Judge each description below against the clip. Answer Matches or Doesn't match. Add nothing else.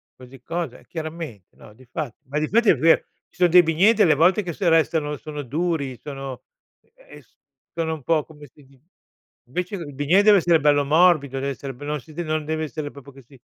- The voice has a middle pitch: Matches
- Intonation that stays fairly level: Doesn't match